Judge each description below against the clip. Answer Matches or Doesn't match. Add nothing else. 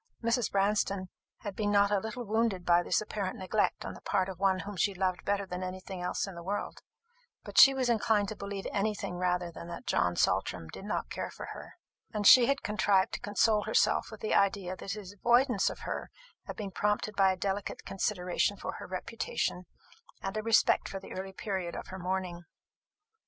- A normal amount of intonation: Doesn't match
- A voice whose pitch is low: Doesn't match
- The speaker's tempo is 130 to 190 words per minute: Doesn't match